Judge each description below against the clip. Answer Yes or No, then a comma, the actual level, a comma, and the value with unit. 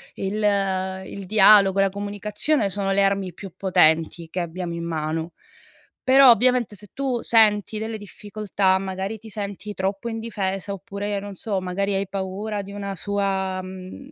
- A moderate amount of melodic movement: No, narrow, 1.8 semitones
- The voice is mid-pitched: No, high, 200 Hz